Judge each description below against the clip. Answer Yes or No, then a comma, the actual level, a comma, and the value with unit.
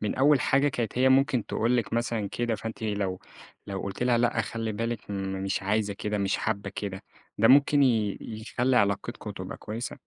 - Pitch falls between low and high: No, low, 110 Hz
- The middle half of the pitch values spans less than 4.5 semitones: Yes, average, 3.3 semitones